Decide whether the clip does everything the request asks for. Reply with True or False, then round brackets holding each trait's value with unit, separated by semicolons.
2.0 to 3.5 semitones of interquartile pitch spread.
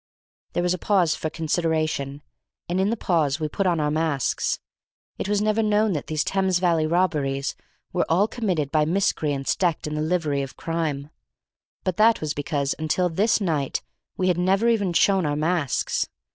False (3.9 semitones)